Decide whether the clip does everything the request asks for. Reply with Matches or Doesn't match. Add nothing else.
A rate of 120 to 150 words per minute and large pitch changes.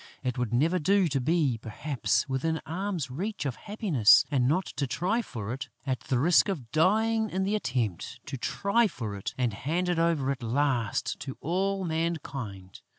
Doesn't match